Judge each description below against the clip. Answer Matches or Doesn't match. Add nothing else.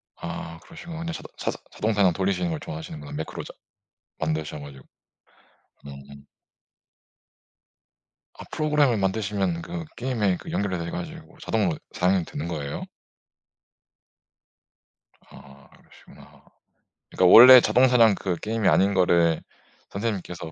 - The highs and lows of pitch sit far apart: Matches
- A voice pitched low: Matches